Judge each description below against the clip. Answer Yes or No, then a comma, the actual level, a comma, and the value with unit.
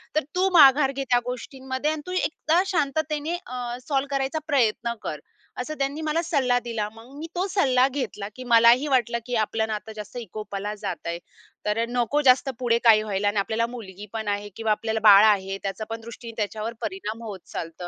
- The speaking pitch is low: No, high, 235 Hz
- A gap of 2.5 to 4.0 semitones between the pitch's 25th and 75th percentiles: No, average, 4.4 semitones